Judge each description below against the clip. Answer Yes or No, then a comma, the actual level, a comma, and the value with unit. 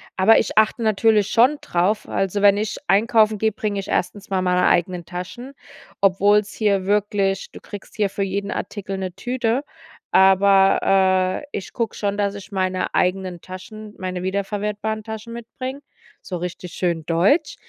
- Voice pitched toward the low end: No, high, 200 Hz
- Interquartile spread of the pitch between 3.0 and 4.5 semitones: No, narrow, 2.4 semitones